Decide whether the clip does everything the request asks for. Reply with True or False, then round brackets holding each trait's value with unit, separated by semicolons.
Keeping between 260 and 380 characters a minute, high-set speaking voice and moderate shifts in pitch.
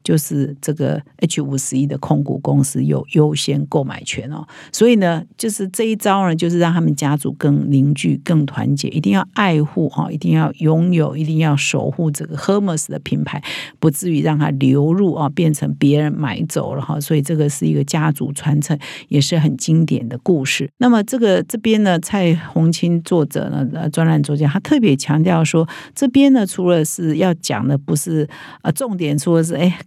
False (295 characters per minute; 155 Hz; 3.1 semitones)